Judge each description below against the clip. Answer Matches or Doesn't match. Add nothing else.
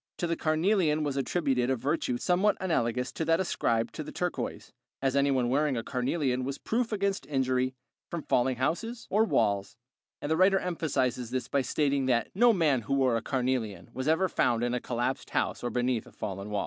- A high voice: Doesn't match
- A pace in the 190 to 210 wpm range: Matches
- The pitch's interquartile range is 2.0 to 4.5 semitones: Doesn't match